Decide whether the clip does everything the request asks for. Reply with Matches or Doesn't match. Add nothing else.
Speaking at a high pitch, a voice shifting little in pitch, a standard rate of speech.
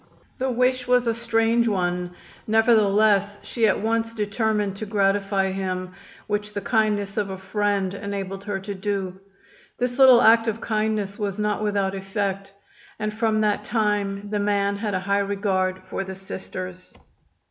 Matches